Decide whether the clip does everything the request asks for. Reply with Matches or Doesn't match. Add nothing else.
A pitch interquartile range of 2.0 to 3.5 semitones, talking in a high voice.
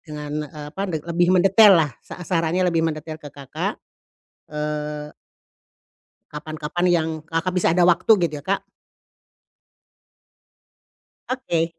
Doesn't match